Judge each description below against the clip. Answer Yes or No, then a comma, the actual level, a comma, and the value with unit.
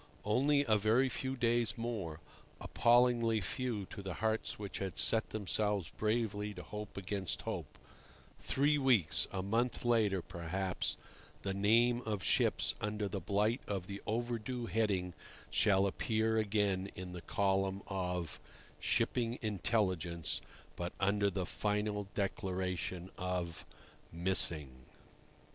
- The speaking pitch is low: Yes, low, 105 Hz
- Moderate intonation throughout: Yes, average, 3.3 semitones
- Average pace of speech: No, slow, 120 wpm